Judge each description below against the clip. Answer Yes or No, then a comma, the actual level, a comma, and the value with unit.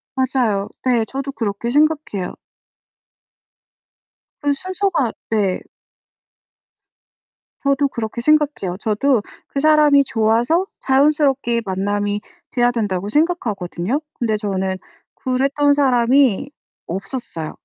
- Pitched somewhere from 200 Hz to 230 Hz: No, high, 245 Hz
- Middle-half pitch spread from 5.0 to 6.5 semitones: Yes, wide, 5.5 semitones